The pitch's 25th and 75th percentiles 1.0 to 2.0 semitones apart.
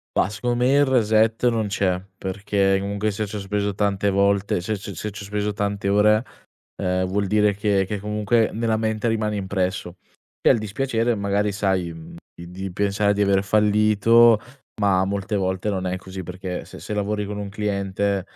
Yes: narrow, 1.7 semitones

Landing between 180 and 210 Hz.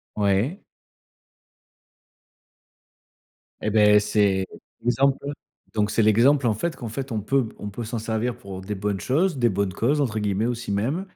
No: low, 110 Hz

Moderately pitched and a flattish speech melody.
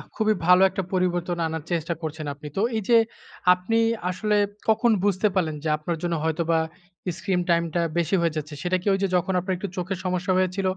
Yes: medium, 180 Hz; narrow, 2.3 semitones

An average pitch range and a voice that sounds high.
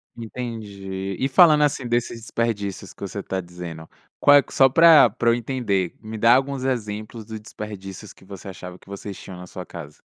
No: average, 4.1 semitones; low, 105 Hz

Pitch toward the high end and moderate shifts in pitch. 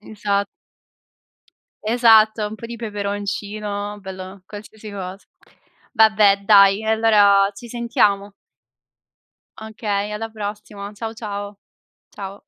No: high, 210 Hz; narrow, 1.5 semitones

